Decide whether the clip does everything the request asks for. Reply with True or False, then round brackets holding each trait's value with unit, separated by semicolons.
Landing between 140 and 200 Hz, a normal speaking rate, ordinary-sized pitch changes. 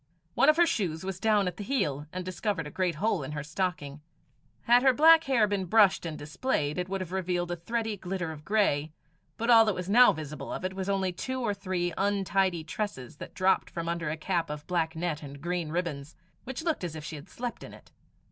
False (185 Hz; 230 wpm; 4.6 semitones)